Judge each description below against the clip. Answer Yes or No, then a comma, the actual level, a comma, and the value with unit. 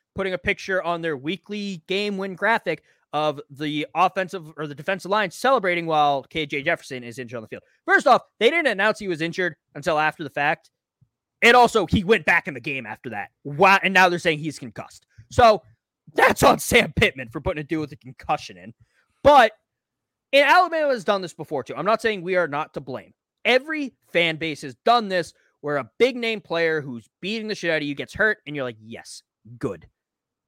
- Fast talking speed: Yes, fast, 215 wpm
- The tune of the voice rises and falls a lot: Yes, wide, 6.2 semitones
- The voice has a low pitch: No, medium, 170 Hz